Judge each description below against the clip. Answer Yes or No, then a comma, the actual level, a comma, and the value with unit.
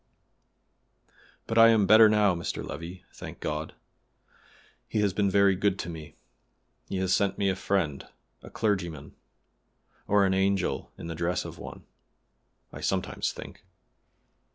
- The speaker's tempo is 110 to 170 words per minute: Yes, average, 145 wpm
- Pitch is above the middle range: No, very low, 95 Hz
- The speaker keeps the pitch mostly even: No, average, 3.1 semitones